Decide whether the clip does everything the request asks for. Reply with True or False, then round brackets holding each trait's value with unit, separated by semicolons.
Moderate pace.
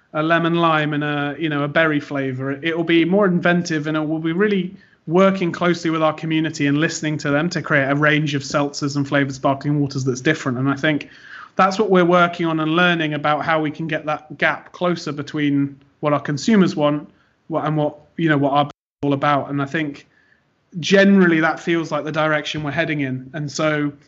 False (220 wpm)